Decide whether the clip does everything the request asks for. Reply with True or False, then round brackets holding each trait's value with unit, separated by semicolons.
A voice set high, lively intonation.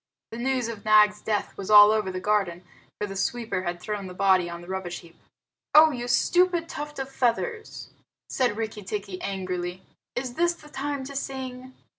True (215 Hz; 5.7 semitones)